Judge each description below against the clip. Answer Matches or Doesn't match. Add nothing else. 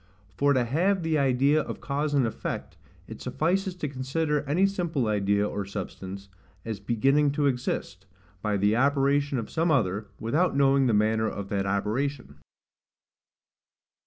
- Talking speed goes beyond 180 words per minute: Doesn't match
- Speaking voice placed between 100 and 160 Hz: Matches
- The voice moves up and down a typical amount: Doesn't match